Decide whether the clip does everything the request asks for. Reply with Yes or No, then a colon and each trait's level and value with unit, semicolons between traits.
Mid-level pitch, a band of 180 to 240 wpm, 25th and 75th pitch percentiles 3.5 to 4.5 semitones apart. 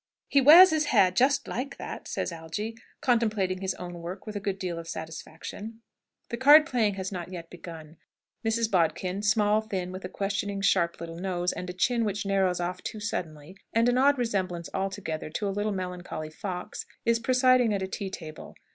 No: high, 195 Hz; average, 190 wpm; average, 4.0 semitones